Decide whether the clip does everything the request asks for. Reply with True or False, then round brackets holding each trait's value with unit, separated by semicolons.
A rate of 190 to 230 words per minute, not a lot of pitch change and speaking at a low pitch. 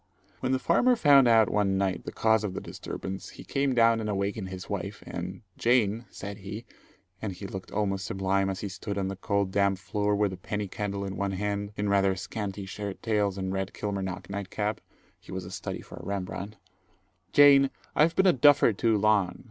True (205 wpm; 2.3 semitones; 100 Hz)